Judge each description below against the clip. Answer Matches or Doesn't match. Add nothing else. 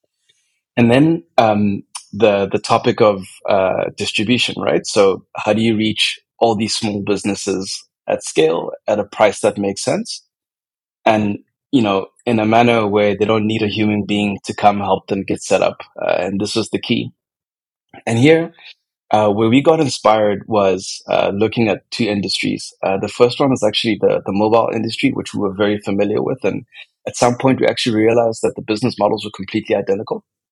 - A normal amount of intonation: Doesn't match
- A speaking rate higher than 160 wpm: Matches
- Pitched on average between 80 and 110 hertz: Matches